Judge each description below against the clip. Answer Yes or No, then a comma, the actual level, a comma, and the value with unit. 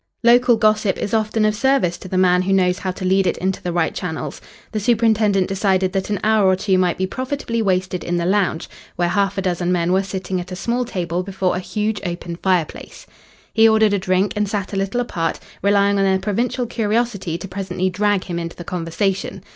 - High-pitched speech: Yes, high, 195 Hz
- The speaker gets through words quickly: Yes, fast, 220 wpm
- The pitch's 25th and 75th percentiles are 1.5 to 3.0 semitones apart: Yes, narrow, 2.6 semitones